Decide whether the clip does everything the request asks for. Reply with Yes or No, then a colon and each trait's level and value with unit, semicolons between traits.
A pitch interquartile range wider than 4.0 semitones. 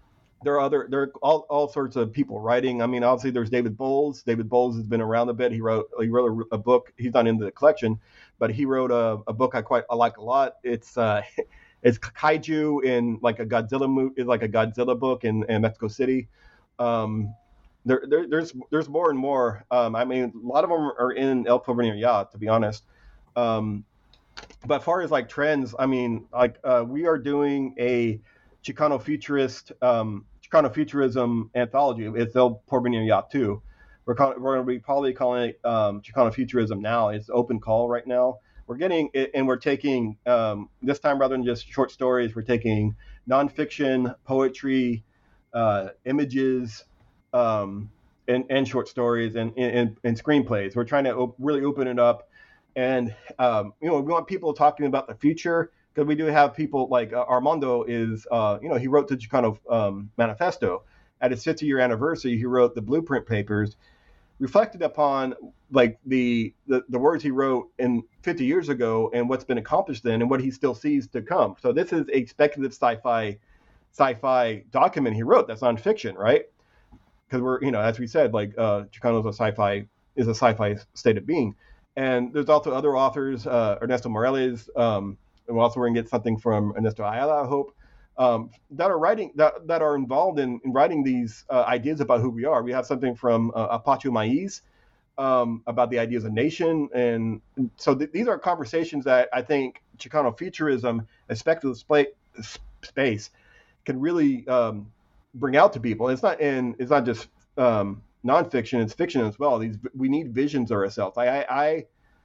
No: average, 3.3 semitones